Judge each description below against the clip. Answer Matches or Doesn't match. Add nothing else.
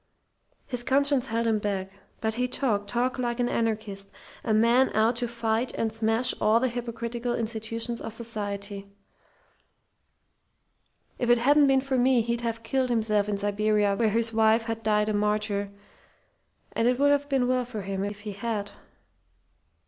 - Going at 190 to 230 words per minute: Doesn't match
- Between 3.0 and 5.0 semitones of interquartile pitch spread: Doesn't match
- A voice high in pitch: Matches